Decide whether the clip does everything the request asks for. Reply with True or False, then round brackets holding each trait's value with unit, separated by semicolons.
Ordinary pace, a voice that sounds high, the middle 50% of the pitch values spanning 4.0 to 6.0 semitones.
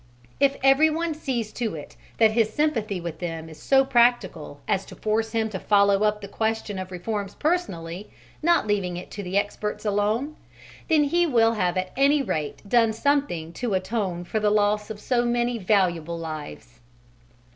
True (170 wpm; 210 Hz; 4.7 semitones)